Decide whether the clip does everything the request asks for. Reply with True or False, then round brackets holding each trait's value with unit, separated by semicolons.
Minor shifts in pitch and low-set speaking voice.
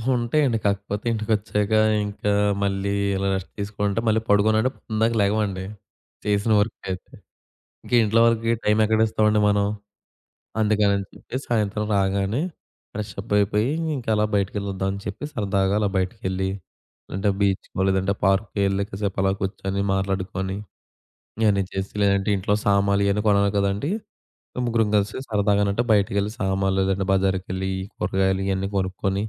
True (1.6 semitones; 100 Hz)